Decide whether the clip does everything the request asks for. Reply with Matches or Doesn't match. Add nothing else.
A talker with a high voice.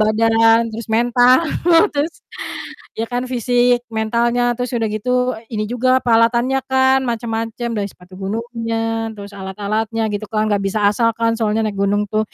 Matches